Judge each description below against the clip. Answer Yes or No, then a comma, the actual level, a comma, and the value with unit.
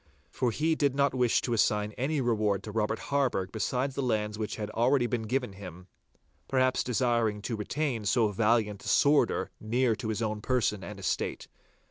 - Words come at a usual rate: Yes, average, 180 wpm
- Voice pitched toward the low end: Yes, low, 115 Hz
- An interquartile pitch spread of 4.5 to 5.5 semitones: No, average, 3.4 semitones